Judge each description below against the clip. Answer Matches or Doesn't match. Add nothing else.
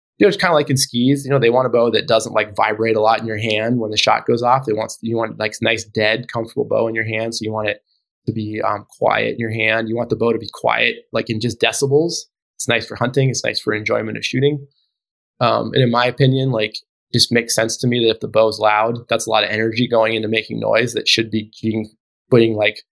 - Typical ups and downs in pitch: Doesn't match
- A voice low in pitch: Matches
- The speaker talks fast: Matches